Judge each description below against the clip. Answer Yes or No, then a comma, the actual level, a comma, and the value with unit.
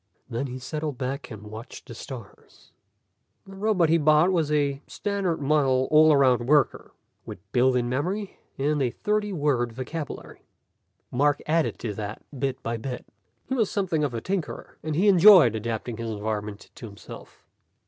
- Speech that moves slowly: No, average, 165 wpm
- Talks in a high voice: No, medium, 140 Hz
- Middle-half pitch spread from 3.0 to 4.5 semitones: No, average, 5.2 semitones